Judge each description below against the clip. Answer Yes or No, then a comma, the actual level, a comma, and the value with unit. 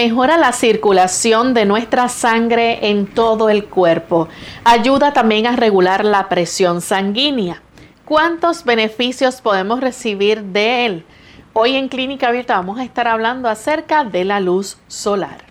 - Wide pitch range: No, average, 3.7 semitones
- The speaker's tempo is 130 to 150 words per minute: Yes, average, 140 wpm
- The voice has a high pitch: Yes, high, 225 Hz